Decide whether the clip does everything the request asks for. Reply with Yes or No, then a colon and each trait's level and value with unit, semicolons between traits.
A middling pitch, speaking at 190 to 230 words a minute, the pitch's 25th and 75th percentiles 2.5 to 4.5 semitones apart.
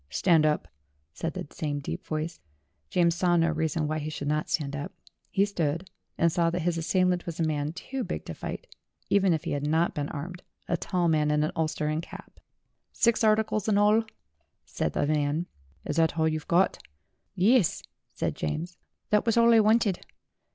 Yes: medium, 165 Hz; average, 195 wpm; average, 3.4 semitones